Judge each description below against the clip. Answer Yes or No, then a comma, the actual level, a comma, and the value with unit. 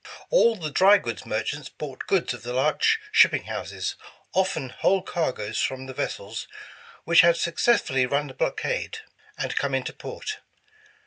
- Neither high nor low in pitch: Yes, medium, 150 Hz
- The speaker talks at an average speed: Yes, average, 150 wpm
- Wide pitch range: Yes, wide, 6.9 semitones